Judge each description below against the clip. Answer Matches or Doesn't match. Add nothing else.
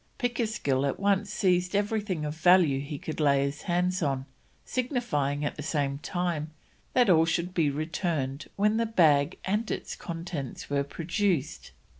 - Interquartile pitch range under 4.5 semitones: Doesn't match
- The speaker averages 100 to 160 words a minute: Matches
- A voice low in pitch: Doesn't match